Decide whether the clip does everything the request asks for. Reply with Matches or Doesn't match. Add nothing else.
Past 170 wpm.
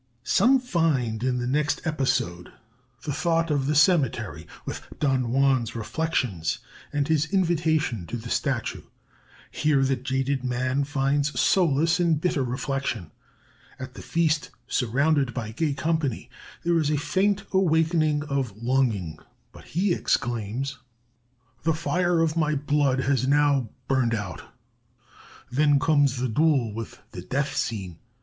Doesn't match